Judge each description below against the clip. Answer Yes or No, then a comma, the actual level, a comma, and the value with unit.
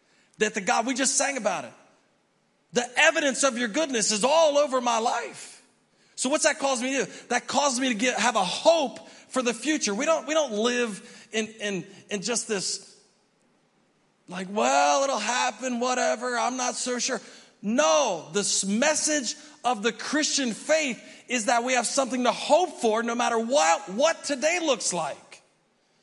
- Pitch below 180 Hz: No, high, 245 Hz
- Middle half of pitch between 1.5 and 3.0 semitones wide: No, average, 4.2 semitones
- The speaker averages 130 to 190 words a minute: Yes, average, 180 wpm